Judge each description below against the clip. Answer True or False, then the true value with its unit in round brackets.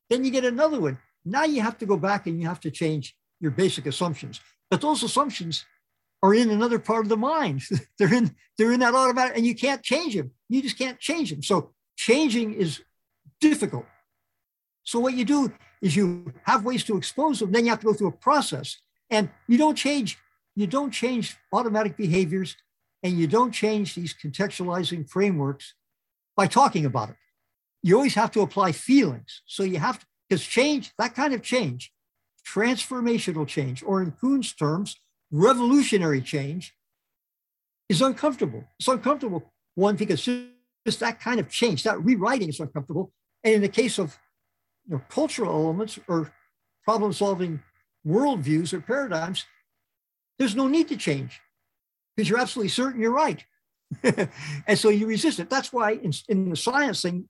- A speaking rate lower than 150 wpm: False (175 wpm)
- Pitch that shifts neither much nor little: False (6.2 semitones)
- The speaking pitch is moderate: False (215 Hz)